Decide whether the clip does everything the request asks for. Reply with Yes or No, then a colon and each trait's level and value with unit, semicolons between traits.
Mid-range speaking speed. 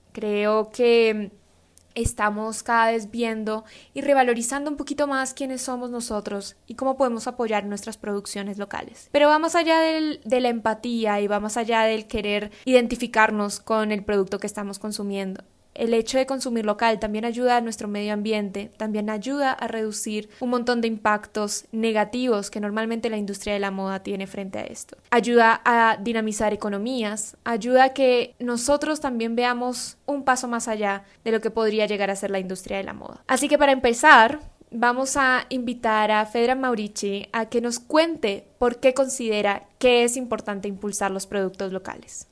Yes: average, 170 wpm